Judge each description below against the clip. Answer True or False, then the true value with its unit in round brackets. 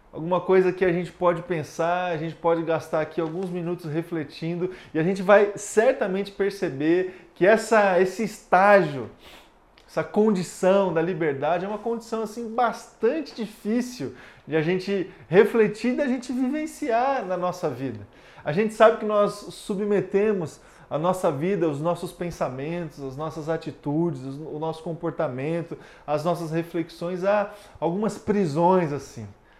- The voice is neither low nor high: True (180 Hz)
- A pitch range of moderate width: True (4.1 semitones)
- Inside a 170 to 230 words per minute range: False (145 wpm)